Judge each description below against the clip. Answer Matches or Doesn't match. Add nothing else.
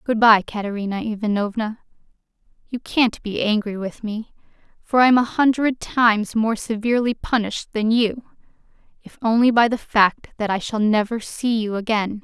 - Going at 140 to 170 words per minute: Matches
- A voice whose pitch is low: Doesn't match